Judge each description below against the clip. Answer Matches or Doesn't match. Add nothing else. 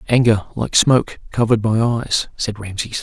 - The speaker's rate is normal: Matches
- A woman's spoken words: Doesn't match